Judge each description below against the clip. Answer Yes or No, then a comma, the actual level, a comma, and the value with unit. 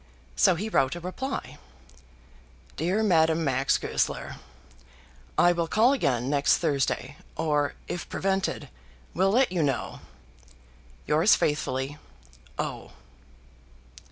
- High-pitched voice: No, medium, 160 Hz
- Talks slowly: Yes, slow, 105 wpm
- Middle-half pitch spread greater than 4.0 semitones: Yes, average, 5.2 semitones